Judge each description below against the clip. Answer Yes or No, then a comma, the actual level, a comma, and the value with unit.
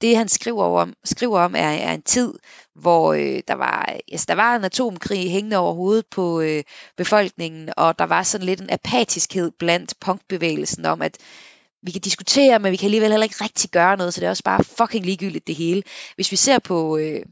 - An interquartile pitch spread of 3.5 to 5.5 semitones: Yes, average, 4.2 semitones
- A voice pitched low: No, high, 190 Hz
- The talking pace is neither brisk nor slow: Yes, average, 215 wpm